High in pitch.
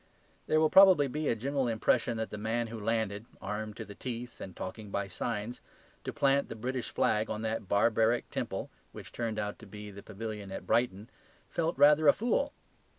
No: low, 115 Hz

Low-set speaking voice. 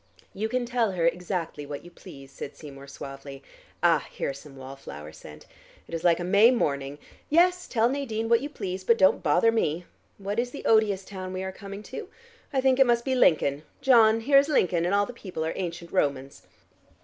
No: high, 190 Hz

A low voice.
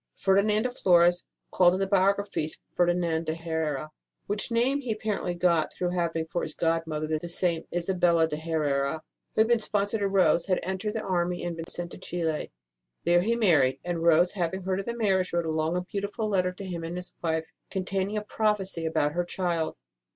No: medium, 175 Hz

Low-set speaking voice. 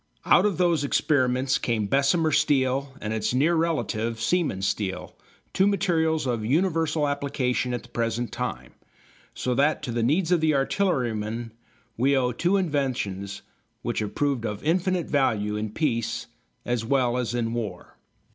Yes: low, 130 Hz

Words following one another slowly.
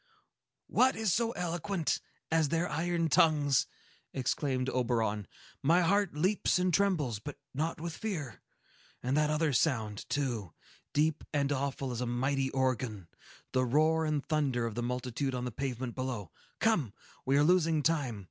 No: average, 150 wpm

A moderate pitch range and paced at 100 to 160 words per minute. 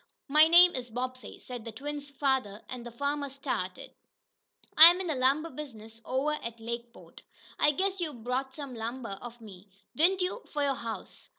No: average, 4.2 semitones; average, 175 wpm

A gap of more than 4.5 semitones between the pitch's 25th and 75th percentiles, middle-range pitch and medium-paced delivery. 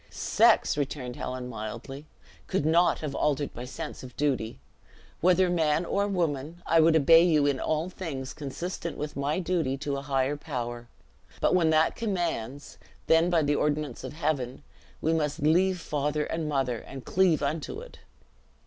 No: average, 3.5 semitones; medium, 150 Hz; average, 165 wpm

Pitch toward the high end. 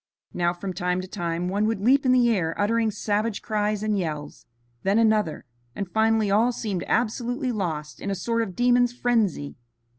Yes: high, 210 Hz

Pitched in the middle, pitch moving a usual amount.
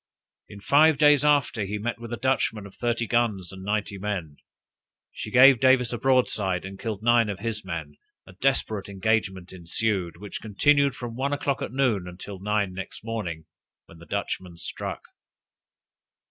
No: low, 105 Hz; average, 4.3 semitones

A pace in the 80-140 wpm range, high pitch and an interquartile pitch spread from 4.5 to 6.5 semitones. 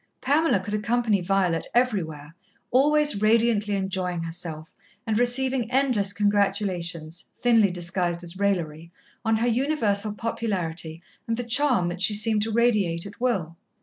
Yes: slow, 135 wpm; high, 205 Hz; average, 5.1 semitones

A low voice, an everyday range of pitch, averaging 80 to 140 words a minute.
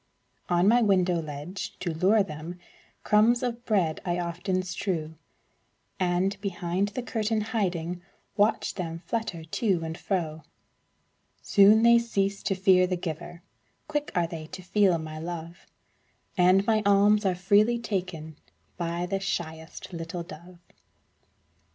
No: medium, 185 Hz; average, 3.2 semitones; slow, 135 wpm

